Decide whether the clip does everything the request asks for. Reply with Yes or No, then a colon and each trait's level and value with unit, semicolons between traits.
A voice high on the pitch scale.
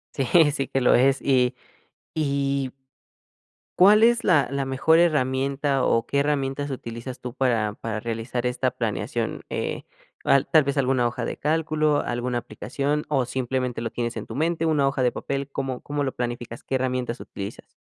No: low, 135 Hz